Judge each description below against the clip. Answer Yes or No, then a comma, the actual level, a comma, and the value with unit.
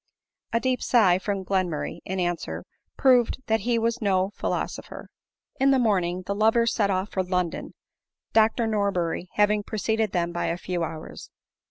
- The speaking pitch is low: No, high, 200 Hz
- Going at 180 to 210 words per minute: No, average, 165 wpm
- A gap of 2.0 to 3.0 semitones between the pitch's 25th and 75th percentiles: No, average, 3.6 semitones